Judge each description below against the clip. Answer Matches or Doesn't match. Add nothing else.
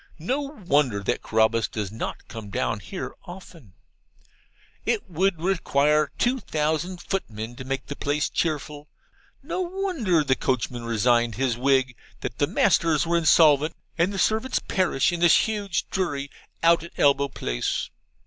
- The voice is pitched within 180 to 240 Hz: Doesn't match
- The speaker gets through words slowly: Doesn't match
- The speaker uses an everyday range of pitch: Doesn't match